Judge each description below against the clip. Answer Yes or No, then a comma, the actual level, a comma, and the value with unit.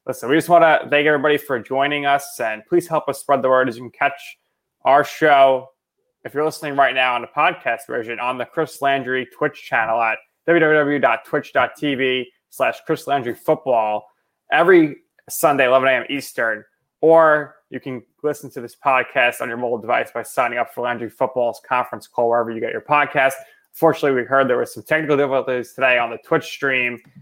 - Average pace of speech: Yes, average, 190 wpm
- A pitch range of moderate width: Yes, average, 3.1 semitones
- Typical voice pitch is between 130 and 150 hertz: Yes, low, 135 Hz